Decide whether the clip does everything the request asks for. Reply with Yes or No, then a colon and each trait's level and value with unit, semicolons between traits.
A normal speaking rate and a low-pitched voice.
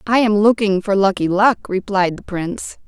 No: average, 190 wpm; high, 200 Hz